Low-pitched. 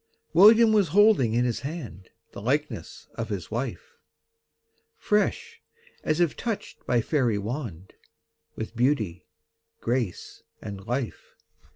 Yes: low, 125 Hz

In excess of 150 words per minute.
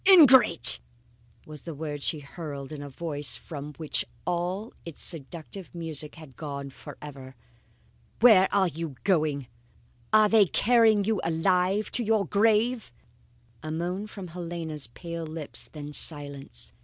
No: slow, 135 wpm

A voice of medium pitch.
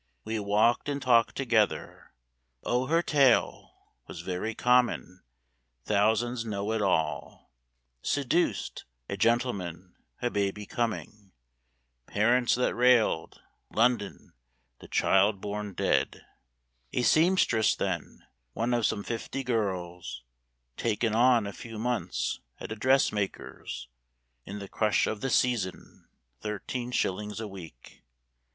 No: low, 110 Hz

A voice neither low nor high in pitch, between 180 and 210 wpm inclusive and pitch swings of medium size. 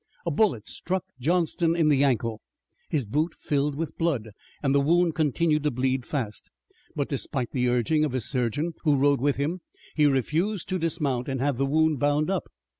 Yes: medium, 145 Hz; average, 190 wpm; average, 3.7 semitones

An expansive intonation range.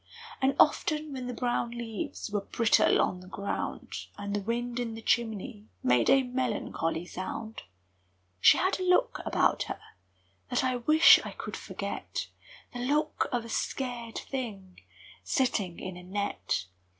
No: average, 4.3 semitones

